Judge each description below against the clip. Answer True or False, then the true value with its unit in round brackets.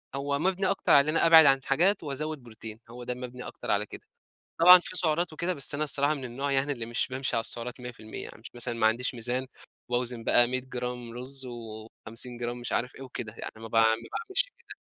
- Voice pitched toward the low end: True (125 Hz)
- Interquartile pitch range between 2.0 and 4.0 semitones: True (3.3 semitones)